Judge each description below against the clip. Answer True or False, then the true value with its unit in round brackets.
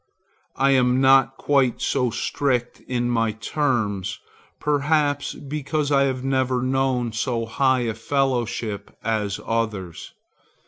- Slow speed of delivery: True (120 wpm)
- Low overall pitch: True (130 Hz)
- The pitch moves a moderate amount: True (3.2 semitones)